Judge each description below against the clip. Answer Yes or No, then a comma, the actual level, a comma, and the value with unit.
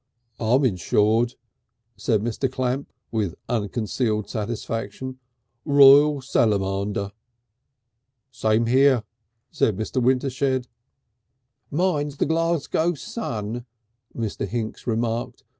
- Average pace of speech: No, slow, 85 wpm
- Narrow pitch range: No, average, 3.9 semitones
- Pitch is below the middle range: Yes, low, 120 Hz